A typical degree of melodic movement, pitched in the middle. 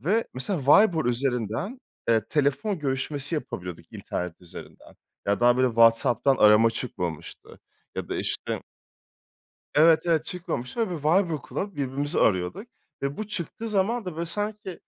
No: wide, 7.8 semitones; medium, 145 Hz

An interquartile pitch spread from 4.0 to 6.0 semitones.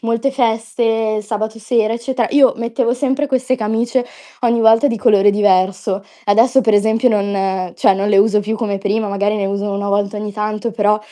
No: narrow, 2.4 semitones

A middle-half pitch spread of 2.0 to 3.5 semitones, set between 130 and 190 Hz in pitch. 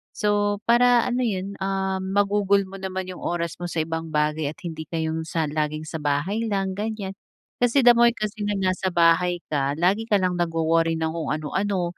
No: average, 3.9 semitones; medium, 185 Hz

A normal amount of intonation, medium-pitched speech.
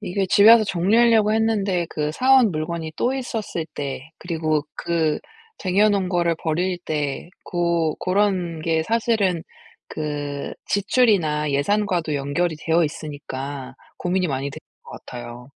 Yes: average, 5.0 semitones; medium, 170 Hz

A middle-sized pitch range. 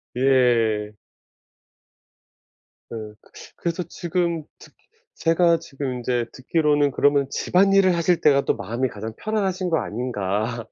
No: wide, 6.4 semitones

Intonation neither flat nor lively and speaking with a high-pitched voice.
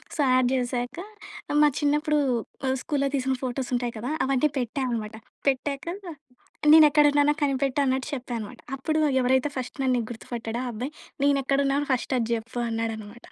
Yes: average, 3.0 semitones; very high, 260 Hz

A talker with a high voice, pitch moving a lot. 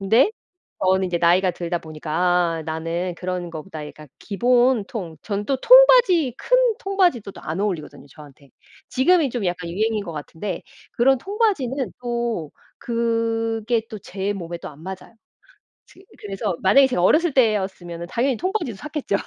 Yes: high, 205 Hz; wide, 6.2 semitones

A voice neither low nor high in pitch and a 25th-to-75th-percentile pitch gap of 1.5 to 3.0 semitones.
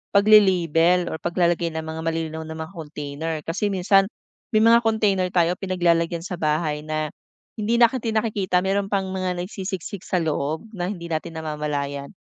No: medium, 175 Hz; average, 3.5 semitones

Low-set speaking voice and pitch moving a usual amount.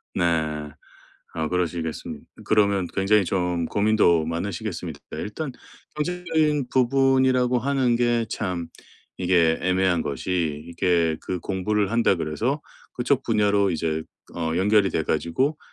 No: very low, 95 Hz; wide, 6.1 semitones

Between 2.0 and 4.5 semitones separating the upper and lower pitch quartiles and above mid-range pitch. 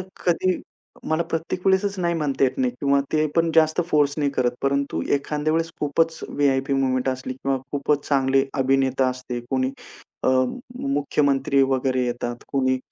No: average, 2.8 semitones; medium, 140 Hz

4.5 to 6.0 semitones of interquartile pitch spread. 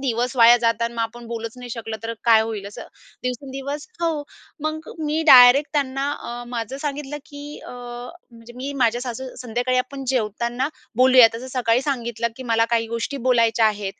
No: average, 2.8 semitones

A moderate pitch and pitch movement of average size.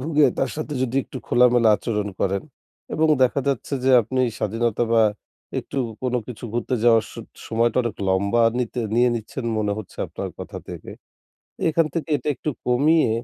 No: low, 120 Hz; average, 3.0 semitones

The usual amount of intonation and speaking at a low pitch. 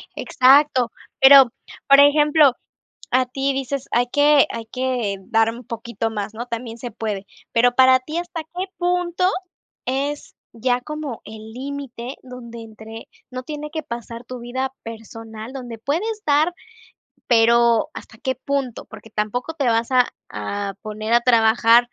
No: average, 3.6 semitones; high, 245 Hz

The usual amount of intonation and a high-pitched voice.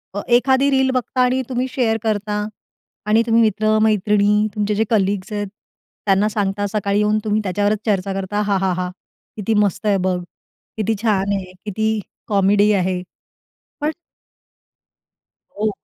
No: narrow, 1.8 semitones; high, 210 Hz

